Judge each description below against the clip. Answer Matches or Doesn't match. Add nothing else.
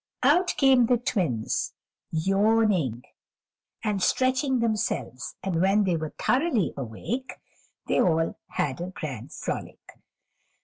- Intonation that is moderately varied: Doesn't match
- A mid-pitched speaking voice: Doesn't match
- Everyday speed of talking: Doesn't match